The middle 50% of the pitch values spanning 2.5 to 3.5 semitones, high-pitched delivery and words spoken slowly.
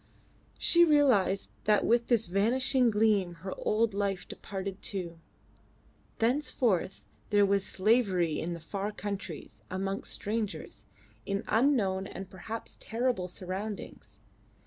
Yes: average, 3.1 semitones; high, 200 Hz; slow, 115 wpm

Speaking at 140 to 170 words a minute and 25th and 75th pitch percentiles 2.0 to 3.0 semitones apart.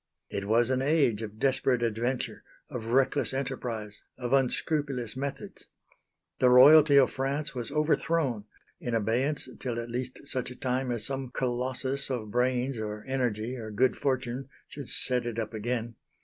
Yes: average, 155 wpm; narrow, 2.5 semitones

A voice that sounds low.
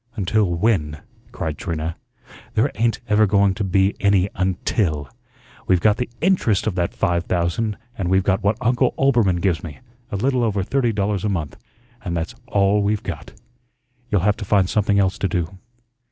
Yes: low, 100 Hz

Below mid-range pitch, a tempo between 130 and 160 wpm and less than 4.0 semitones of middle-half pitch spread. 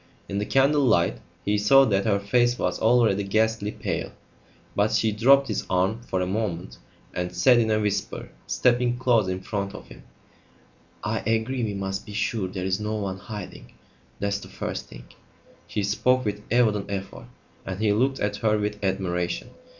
No: low, 105 Hz; average, 175 wpm; average, 2.8 semitones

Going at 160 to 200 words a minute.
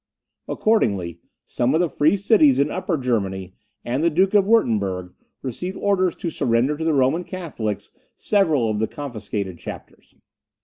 No: average, 150 wpm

